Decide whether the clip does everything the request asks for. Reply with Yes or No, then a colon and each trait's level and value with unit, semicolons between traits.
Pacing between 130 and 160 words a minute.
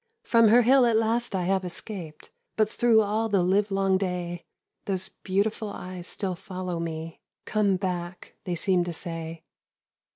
Yes: average, 155 wpm